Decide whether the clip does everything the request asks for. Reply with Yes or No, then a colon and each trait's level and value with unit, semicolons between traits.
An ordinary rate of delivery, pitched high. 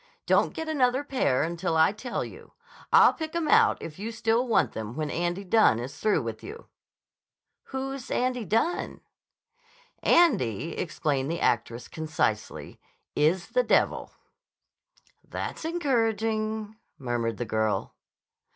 No: slow, 130 wpm; high, 210 Hz